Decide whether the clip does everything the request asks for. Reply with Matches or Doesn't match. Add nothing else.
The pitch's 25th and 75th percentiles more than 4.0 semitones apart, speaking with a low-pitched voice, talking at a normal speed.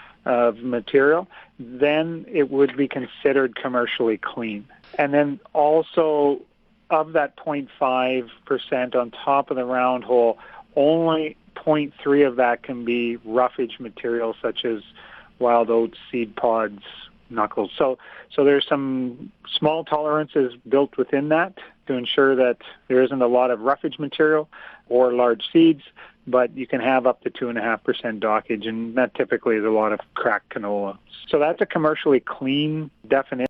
Doesn't match